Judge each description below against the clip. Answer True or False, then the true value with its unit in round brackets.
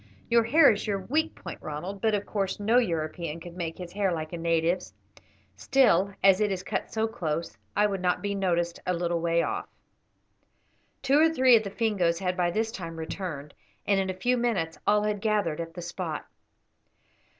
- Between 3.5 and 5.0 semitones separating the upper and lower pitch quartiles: True (4.0 semitones)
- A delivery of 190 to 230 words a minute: True (195 wpm)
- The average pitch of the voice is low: False (190 Hz)